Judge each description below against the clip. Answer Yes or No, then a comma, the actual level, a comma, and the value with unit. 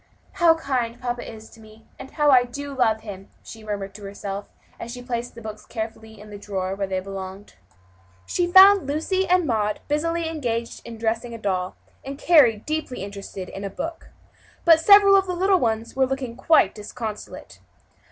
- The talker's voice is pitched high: Yes, high, 230 Hz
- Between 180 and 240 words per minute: Yes, average, 185 wpm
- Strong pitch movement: Yes, wide, 6.2 semitones